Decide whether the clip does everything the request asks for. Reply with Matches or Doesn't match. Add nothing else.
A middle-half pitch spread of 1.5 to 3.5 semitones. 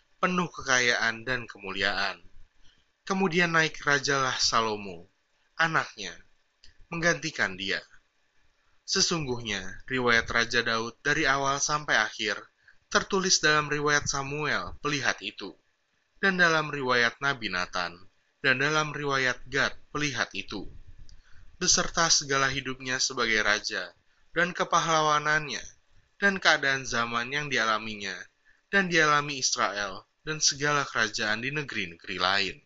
Doesn't match